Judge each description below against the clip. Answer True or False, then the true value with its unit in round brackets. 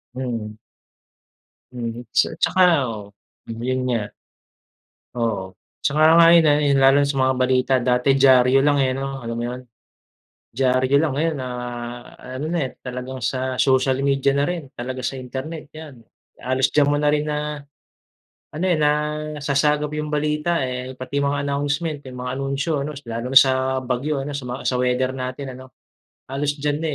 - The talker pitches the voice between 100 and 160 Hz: True (135 Hz)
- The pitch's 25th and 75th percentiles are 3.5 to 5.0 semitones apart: False (2.5 semitones)